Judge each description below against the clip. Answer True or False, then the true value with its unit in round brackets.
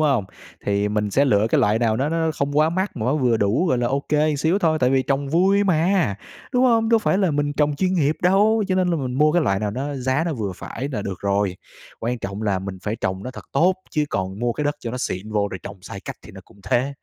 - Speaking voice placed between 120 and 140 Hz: True (135 Hz)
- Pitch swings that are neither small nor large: False (7.4 semitones)